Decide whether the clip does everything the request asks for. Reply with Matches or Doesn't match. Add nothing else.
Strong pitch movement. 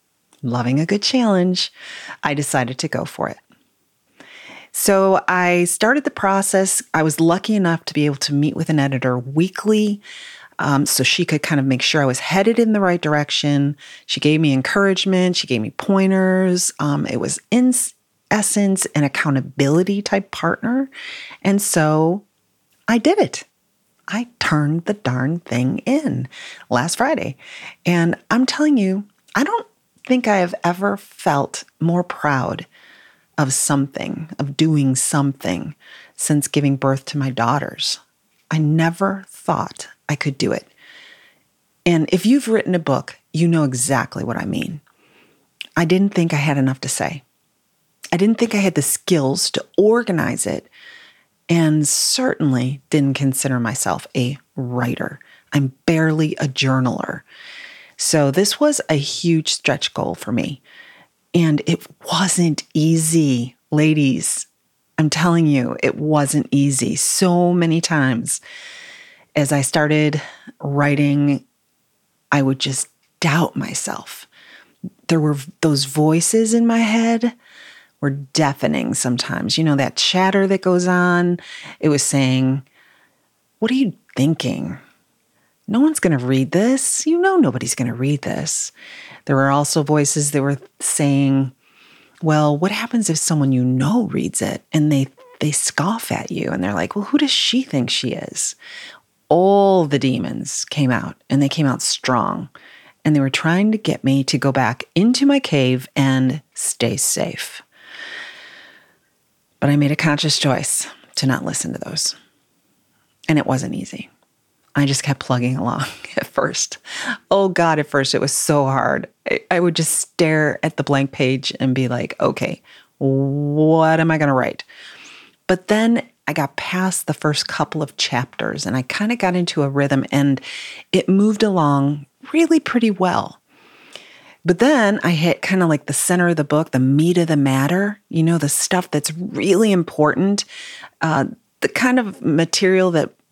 Matches